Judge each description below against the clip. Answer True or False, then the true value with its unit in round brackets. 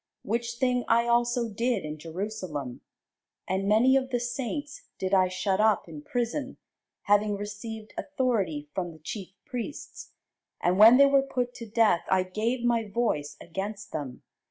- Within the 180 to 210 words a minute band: False (155 wpm)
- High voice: True (215 Hz)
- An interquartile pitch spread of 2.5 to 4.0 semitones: False (4.5 semitones)